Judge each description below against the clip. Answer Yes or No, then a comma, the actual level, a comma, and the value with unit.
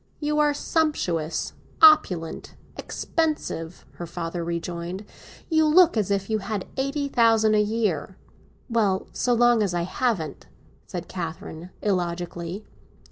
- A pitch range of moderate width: No, wide, 6.3 semitones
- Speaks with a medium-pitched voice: No, high, 200 Hz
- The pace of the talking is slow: Yes, slow, 125 wpm